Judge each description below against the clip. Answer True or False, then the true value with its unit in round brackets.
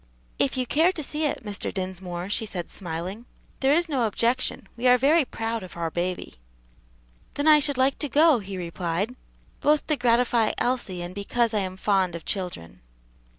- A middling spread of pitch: False (6.3 semitones)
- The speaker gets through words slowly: False (185 wpm)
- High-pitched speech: True (225 Hz)